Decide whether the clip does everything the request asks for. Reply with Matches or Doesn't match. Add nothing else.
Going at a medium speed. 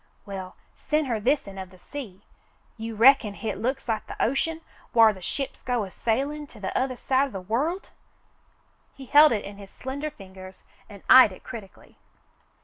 Matches